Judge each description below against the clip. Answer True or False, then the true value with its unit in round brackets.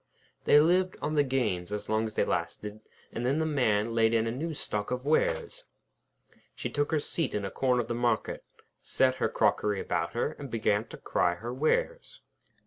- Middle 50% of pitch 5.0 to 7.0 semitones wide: True (5.6 semitones)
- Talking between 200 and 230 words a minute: True (205 wpm)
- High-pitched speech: False (125 Hz)